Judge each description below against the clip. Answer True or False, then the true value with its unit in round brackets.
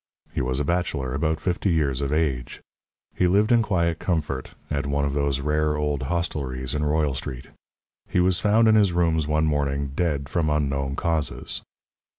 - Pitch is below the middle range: True (75 Hz)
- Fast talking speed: False (175 wpm)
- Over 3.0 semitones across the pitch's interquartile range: True (3.5 semitones)